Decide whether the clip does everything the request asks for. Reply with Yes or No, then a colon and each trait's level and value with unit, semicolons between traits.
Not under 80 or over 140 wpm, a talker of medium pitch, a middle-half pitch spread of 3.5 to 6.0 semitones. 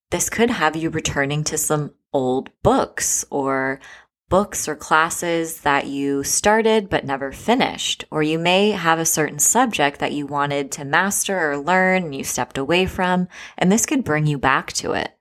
No: average, 180 wpm; medium, 155 Hz; average, 4.4 semitones